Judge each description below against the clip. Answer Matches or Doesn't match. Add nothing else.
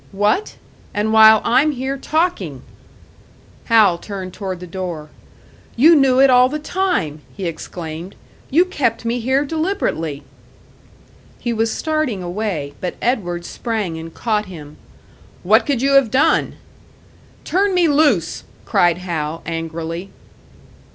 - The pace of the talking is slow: Matches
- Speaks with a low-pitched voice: Doesn't match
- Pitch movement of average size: Doesn't match